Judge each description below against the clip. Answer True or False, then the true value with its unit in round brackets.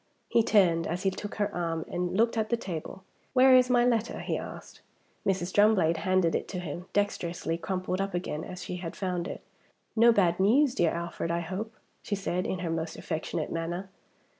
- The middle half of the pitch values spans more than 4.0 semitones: False (3.5 semitones)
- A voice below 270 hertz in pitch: True (185 Hz)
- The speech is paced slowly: False (195 wpm)